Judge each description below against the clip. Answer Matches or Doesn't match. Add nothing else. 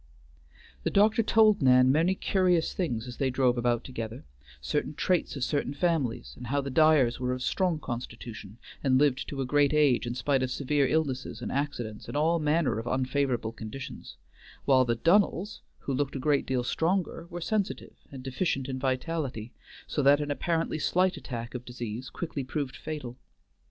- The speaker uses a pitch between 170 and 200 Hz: Doesn't match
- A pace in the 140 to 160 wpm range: Doesn't match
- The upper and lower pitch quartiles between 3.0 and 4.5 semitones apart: Matches